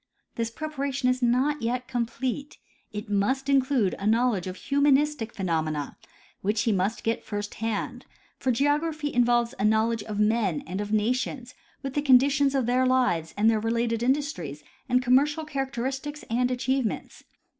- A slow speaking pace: No, average, 155 wpm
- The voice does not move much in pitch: No, average, 4.0 semitones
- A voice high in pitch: Yes, high, 245 Hz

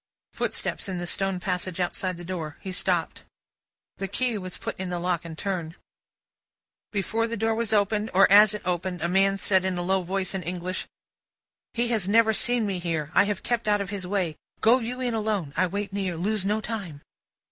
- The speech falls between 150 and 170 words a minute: No, fast, 205 wpm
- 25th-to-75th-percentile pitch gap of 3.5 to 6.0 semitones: No, average, 2.9 semitones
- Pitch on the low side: No, high, 190 Hz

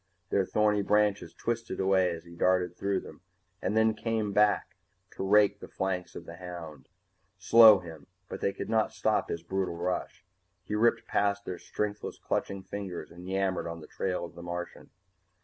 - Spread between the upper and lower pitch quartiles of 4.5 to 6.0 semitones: No, average, 3.0 semitones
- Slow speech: No, average, 175 wpm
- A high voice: No, very low, 95 Hz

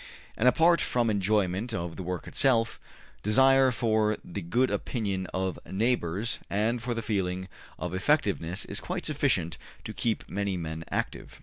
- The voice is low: Yes, low, 105 Hz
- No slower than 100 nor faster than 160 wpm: Yes, average, 150 wpm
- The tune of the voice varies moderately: Yes, average, 4.7 semitones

